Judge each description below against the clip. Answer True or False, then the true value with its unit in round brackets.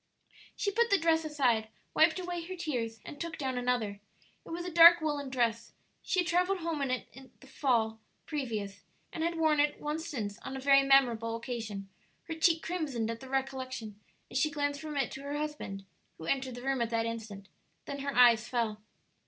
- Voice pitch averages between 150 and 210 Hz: False (270 Hz)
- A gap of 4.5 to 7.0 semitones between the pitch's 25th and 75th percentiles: True (5.3 semitones)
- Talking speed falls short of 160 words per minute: False (200 wpm)